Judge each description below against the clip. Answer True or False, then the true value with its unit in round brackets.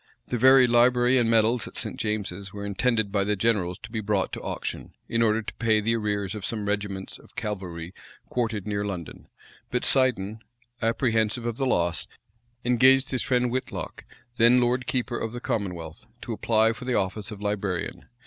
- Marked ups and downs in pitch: False (3.2 semitones)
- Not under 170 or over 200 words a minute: True (180 wpm)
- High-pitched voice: False (110 Hz)